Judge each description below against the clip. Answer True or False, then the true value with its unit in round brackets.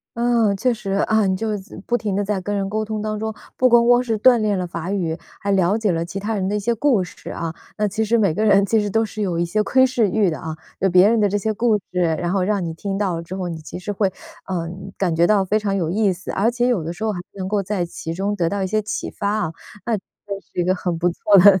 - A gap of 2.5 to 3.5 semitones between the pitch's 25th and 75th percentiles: True (3.0 semitones)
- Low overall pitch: False (200 Hz)